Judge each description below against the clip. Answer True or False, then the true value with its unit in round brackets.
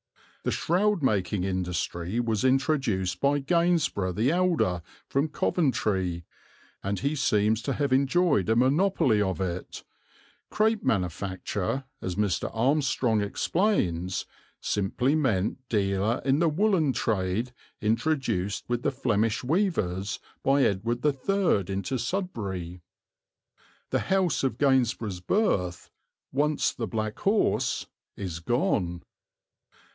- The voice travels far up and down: True (7.1 semitones)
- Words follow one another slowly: True (110 wpm)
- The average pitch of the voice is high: False (115 Hz)